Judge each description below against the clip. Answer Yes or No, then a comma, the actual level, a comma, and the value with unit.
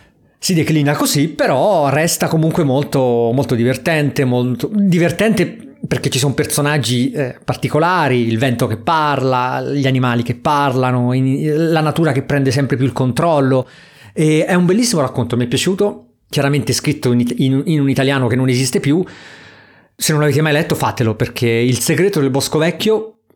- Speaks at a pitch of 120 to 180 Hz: Yes, medium, 140 Hz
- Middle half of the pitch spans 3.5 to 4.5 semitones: Yes, average, 3.8 semitones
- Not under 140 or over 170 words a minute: Yes, average, 165 wpm